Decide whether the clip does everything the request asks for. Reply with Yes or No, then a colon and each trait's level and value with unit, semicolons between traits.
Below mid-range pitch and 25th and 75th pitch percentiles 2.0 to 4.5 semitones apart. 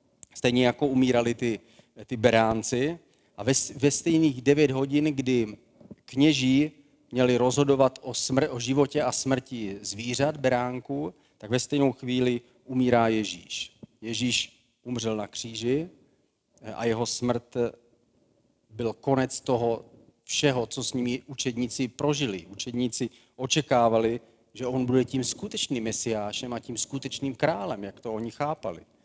Yes: low, 125 Hz; average, 2.7 semitones